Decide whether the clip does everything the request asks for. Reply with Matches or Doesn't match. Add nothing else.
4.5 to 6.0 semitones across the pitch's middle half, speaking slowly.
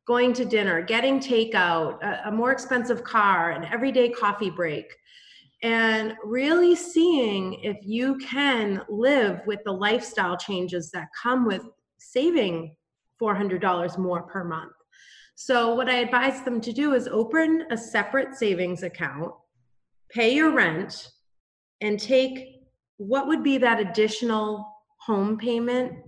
Matches